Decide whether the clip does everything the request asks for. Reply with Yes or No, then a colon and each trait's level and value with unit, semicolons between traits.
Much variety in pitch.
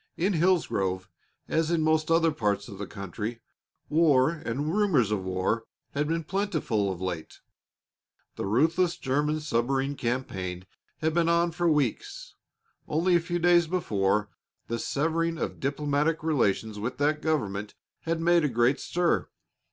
Yes: wide, 7.3 semitones